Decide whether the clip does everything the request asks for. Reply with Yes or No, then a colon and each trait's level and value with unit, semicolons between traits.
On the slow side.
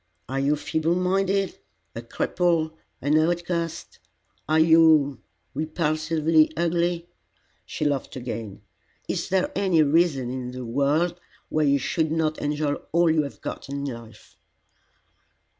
Yes: slow, 125 wpm